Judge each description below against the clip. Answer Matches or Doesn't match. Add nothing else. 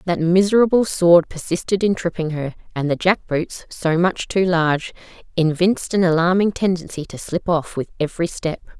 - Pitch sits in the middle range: Matches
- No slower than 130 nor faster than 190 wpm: Matches